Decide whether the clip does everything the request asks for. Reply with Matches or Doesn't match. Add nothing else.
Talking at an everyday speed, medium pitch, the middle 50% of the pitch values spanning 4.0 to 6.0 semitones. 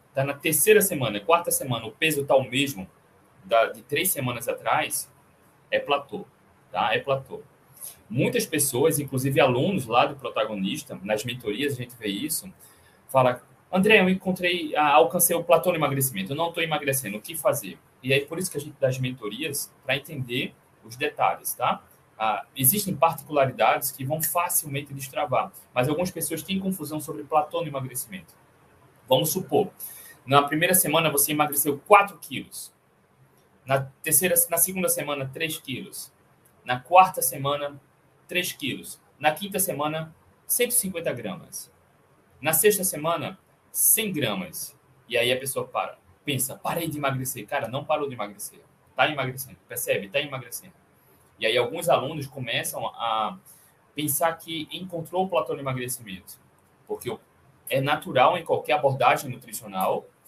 Matches